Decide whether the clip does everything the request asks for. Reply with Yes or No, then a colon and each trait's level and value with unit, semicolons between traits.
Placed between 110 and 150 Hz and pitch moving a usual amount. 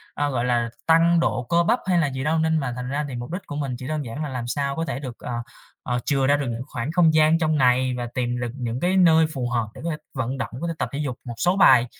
Yes: medium, 140 Hz; average, 4.4 semitones